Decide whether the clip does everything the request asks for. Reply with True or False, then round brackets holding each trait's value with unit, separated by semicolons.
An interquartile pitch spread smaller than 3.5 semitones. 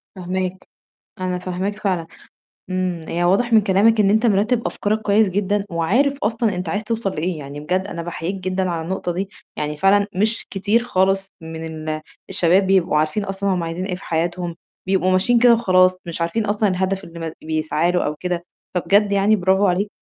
True (3.0 semitones)